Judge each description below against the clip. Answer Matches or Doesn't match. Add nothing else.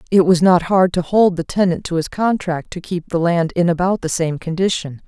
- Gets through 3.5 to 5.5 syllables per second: Matches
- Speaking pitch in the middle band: Matches